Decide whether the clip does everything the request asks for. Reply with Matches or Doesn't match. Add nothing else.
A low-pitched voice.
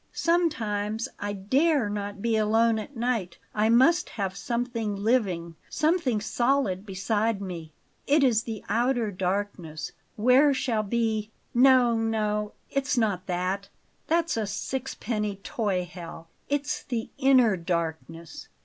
Doesn't match